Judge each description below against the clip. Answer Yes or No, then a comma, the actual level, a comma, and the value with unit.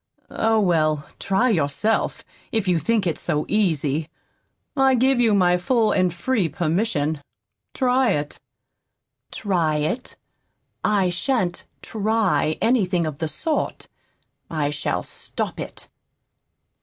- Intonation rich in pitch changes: Yes, wide, 6.2 semitones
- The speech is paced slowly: Yes, slow, 120 wpm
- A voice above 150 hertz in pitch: Yes, medium, 185 Hz